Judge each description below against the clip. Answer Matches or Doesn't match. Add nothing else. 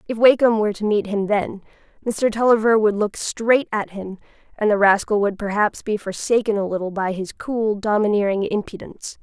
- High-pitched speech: Matches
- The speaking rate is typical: Matches